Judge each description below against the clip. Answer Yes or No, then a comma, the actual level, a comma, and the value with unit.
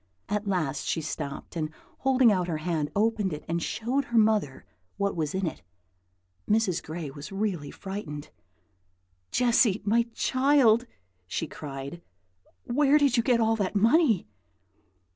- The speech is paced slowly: No, average, 145 wpm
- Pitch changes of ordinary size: No, wide, 6.5 semitones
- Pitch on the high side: Yes, high, 200 Hz